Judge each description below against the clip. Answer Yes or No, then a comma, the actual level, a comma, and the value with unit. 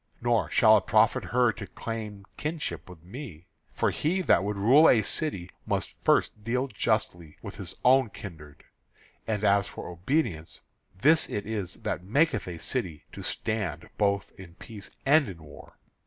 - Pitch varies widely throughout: Yes, wide, 6.0 semitones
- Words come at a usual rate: Yes, average, 165 wpm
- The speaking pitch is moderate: No, low, 105 Hz